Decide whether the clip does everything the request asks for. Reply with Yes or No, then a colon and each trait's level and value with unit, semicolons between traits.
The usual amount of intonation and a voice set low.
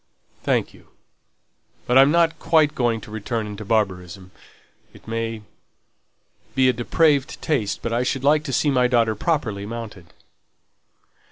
Yes: average, 4.2 semitones; low, 115 Hz